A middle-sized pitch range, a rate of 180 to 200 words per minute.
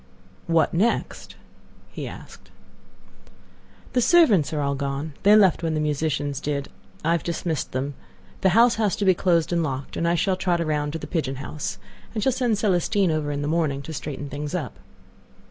Yes: average, 4.5 semitones; average, 185 wpm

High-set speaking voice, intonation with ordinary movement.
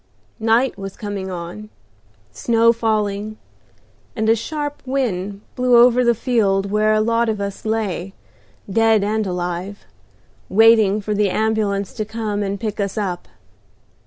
No: high, 215 Hz; narrow, 2.2 semitones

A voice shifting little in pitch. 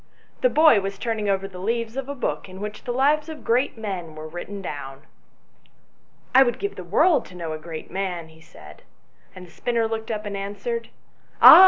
No: wide, 5.6 semitones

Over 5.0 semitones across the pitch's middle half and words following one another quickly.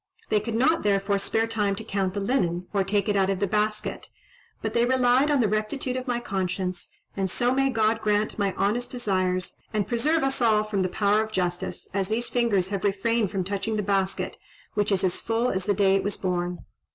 No: average, 3.0 semitones; fast, 220 wpm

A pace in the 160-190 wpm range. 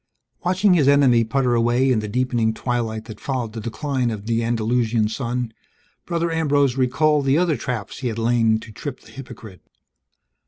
Yes: average, 170 wpm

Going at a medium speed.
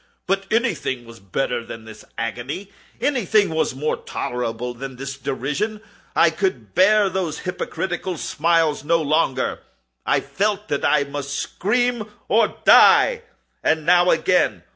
No: slow, 130 wpm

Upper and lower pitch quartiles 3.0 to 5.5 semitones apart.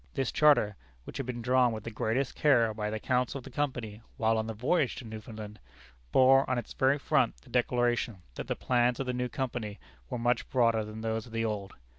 No: narrow, 2.6 semitones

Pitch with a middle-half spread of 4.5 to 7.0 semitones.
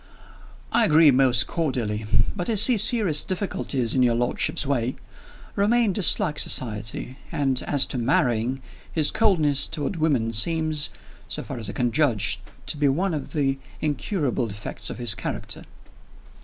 Yes: average, 5.1 semitones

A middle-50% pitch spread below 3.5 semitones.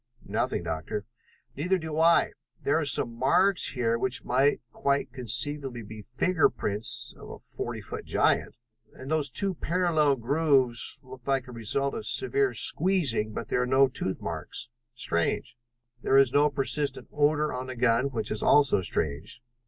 No: average, 4.3 semitones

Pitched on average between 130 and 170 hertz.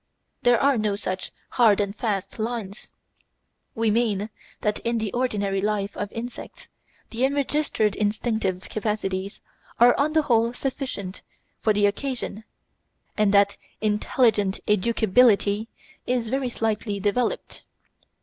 No: high, 215 Hz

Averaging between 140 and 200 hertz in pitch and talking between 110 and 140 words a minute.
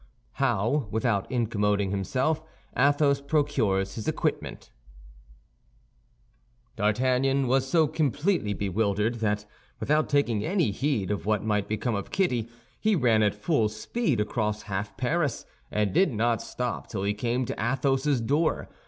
No: low, 120 Hz; slow, 135 wpm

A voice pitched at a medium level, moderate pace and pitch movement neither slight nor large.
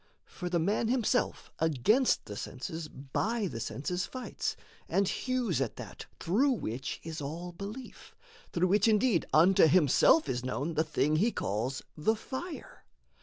No: medium, 175 Hz; average, 150 wpm; wide, 7.0 semitones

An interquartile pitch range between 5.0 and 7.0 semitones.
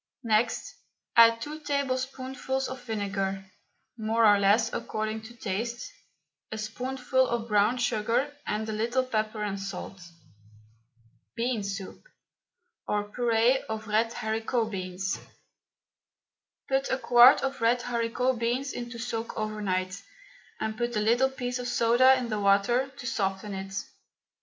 No: average, 3.0 semitones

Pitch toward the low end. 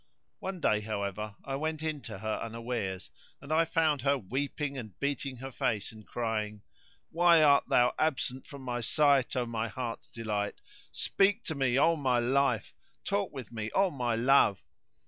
Yes: low, 130 Hz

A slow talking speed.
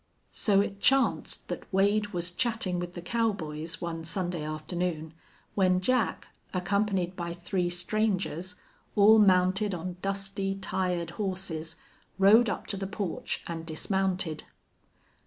Yes: slow, 125 wpm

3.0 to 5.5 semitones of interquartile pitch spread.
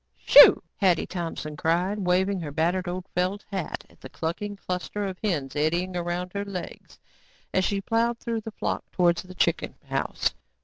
No: narrow, 2.6 semitones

